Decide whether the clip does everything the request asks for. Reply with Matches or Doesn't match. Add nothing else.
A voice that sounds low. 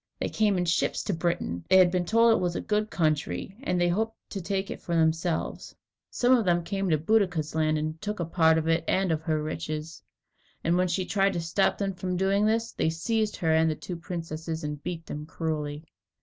Doesn't match